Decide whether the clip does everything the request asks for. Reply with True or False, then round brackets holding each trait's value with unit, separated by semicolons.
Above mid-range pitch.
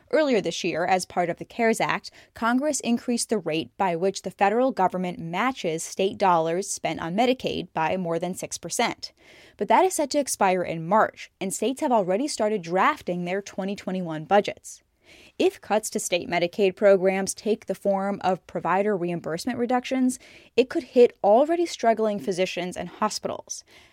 True (200 Hz)